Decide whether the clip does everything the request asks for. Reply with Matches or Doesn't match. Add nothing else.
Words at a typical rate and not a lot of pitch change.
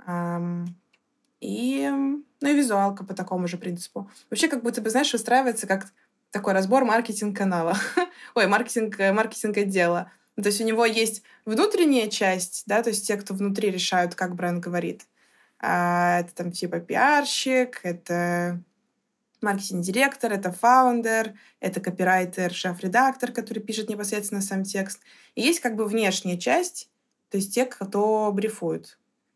Doesn't match